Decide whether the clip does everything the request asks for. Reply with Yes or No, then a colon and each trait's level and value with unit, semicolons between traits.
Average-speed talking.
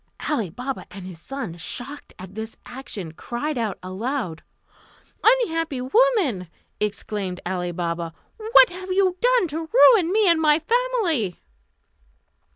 No: slow, 130 wpm